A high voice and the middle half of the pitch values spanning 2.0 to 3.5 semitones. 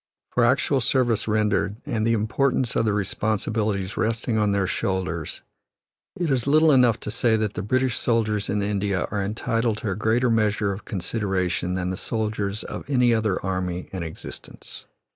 No: low, 105 Hz; average, 2.7 semitones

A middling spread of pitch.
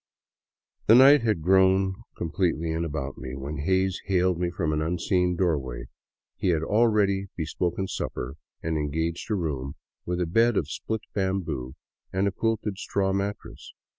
Yes: average, 3.6 semitones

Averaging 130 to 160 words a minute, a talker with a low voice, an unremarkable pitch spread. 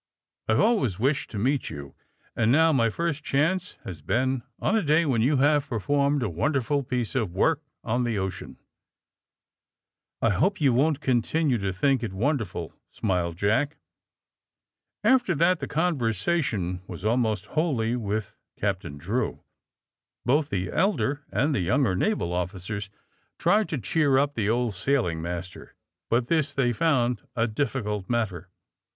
No: average, 155 wpm; low, 120 Hz; wide, 6.3 semitones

